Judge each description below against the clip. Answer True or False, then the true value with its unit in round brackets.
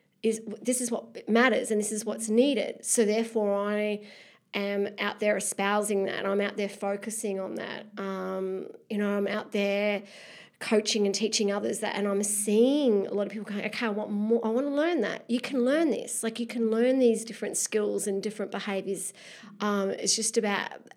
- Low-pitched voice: False (210 Hz)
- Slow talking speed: False (200 wpm)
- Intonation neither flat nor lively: False (1.8 semitones)